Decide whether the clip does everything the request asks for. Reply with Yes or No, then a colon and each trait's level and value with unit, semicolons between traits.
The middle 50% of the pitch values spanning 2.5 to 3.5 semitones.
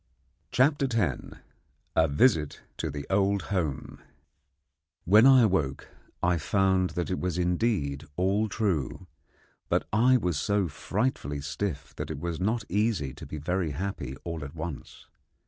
No: average, 5.3 semitones